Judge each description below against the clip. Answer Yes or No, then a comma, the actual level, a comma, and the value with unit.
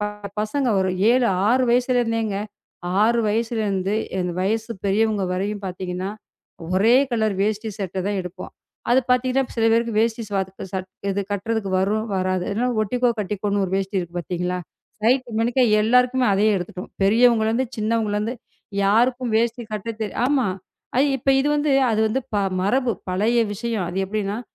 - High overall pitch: Yes, high, 215 Hz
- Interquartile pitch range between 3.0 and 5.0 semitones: Yes, average, 3.4 semitones